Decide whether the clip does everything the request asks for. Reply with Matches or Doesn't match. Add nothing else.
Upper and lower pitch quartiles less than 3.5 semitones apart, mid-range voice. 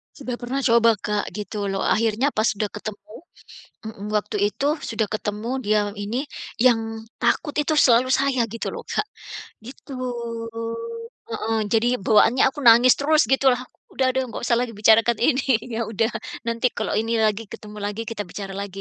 Doesn't match